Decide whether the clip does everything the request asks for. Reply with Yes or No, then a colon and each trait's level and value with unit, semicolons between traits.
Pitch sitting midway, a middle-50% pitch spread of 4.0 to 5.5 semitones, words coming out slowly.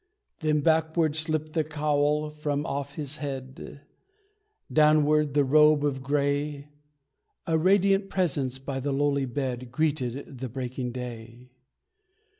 No: medium, 145 Hz; narrow, 2.5 semitones; slow, 120 wpm